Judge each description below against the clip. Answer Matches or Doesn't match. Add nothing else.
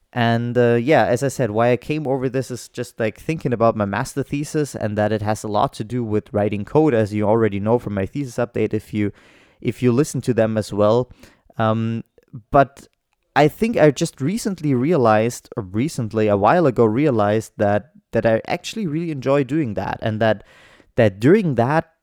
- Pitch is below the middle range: Matches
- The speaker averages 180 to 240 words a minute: Matches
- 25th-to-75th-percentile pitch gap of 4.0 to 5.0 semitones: Matches